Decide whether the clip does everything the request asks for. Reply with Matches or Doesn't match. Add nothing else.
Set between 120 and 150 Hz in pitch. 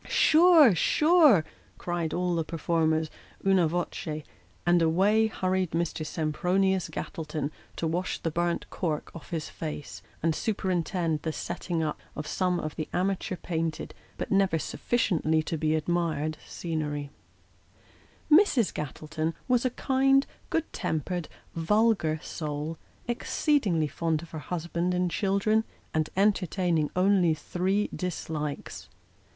Doesn't match